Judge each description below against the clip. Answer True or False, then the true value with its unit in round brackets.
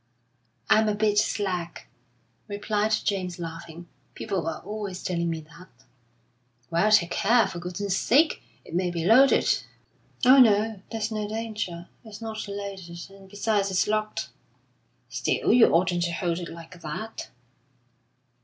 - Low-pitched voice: False (200 Hz)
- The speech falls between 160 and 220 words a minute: False (145 wpm)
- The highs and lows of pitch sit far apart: False (3.8 semitones)